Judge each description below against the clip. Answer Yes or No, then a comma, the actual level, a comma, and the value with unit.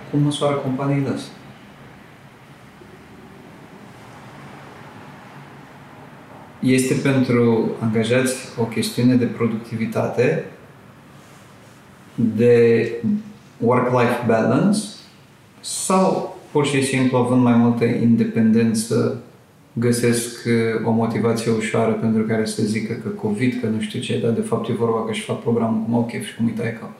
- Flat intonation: Yes, narrow, 2.2 semitones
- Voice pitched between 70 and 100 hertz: No, low, 115 Hz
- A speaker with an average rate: No, slow, 110 wpm